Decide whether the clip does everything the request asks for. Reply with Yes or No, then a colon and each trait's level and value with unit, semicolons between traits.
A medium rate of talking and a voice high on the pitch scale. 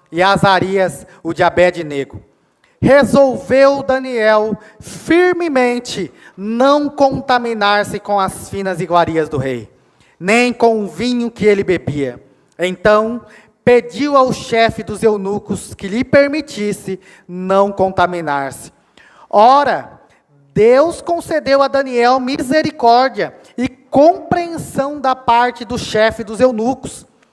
No: slow, 105 wpm; high, 220 Hz